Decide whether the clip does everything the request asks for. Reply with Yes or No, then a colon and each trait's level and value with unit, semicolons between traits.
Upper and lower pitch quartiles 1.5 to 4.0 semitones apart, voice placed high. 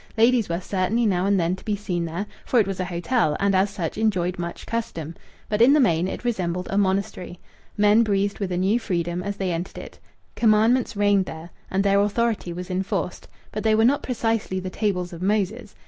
Yes: average, 3.2 semitones; high, 195 Hz